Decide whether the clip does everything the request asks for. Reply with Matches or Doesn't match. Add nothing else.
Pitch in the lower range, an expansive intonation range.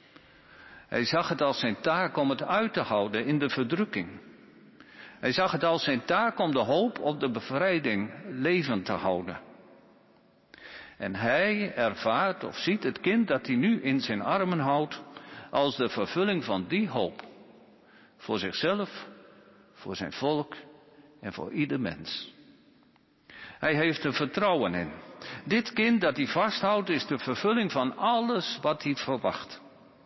Doesn't match